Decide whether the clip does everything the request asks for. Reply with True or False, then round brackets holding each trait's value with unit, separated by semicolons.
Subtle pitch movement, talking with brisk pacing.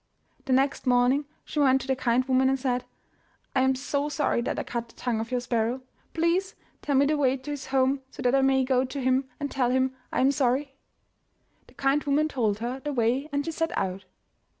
True (2.0 semitones; 225 wpm)